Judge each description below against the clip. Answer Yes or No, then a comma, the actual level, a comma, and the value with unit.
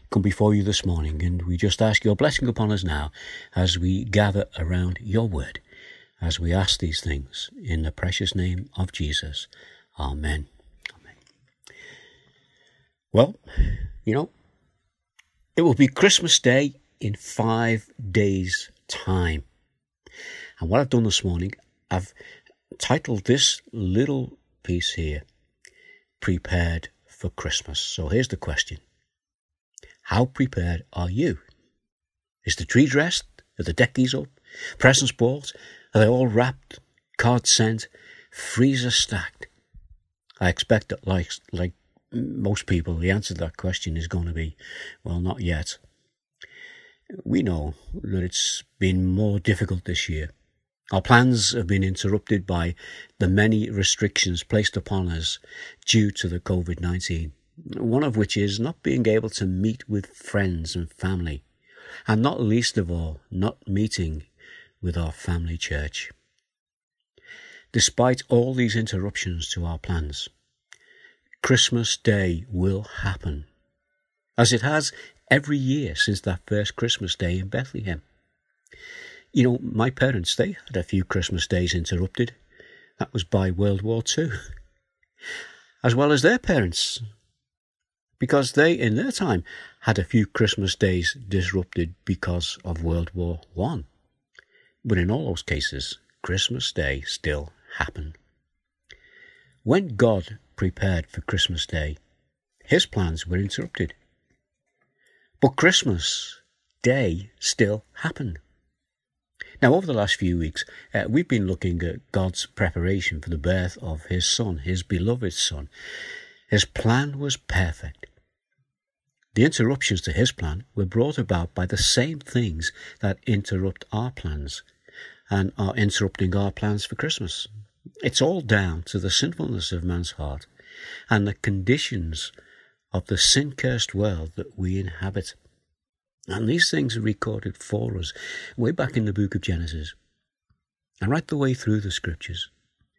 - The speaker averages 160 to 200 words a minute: No, average, 140 wpm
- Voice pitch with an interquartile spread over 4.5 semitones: Yes, average, 5.1 semitones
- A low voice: Yes, low, 100 Hz